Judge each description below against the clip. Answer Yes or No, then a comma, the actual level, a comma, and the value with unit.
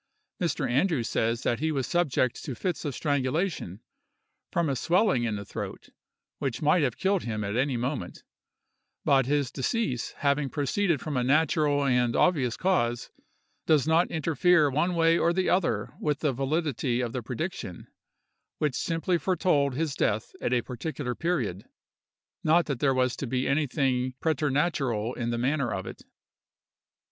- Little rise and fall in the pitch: No, average, 4.6 semitones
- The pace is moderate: Yes, average, 160 wpm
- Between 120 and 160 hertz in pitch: Yes, medium, 140 Hz